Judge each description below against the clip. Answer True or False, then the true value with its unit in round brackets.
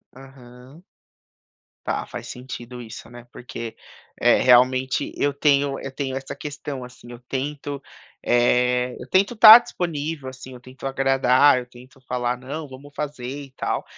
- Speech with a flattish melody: True (2.3 semitones)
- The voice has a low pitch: True (130 Hz)